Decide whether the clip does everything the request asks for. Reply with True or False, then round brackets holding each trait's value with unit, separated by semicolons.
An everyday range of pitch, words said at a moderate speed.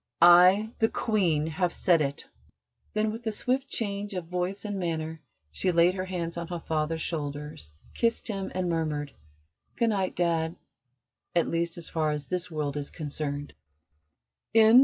True (3.8 semitones; 160 wpm)